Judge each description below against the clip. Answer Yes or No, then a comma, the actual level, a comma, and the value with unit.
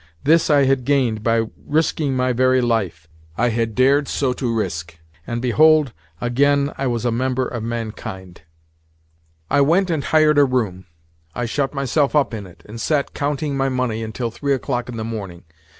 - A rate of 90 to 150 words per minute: No, average, 180 wpm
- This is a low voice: Yes, low, 125 Hz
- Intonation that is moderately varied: Yes, average, 3.7 semitones